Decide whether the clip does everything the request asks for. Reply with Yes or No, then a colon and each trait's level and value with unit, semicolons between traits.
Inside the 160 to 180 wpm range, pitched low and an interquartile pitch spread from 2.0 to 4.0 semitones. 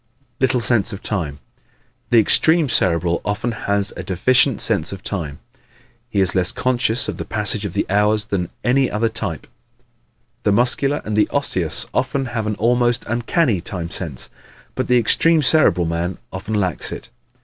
No: average, 170 wpm; low, 105 Hz; average, 4.8 semitones